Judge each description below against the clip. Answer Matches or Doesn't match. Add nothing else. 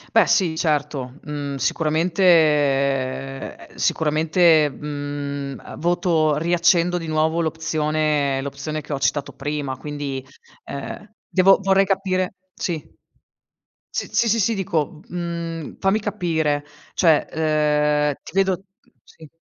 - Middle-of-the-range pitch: Matches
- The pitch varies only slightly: Doesn't match